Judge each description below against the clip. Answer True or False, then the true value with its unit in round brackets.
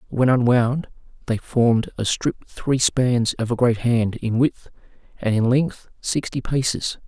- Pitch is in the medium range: False (120 Hz)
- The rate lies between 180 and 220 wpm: False (160 wpm)